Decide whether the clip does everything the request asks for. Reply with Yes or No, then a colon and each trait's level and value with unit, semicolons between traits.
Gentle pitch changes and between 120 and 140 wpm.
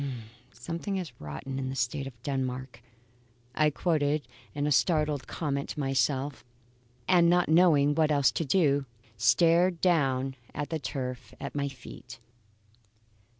No: average, 3.4 semitones; slow, 135 wpm